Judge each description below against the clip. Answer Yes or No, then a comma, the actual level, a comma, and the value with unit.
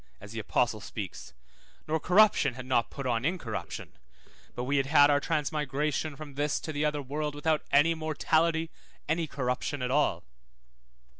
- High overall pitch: No, medium, 145 Hz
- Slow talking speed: No, average, 160 wpm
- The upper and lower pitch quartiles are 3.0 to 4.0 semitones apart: Yes, average, 3.5 semitones